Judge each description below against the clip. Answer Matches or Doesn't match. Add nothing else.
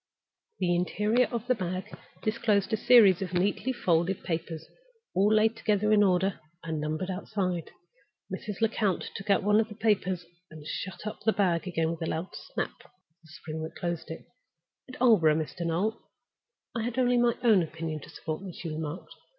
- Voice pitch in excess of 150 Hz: Matches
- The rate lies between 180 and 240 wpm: Matches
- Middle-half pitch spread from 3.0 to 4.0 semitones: Doesn't match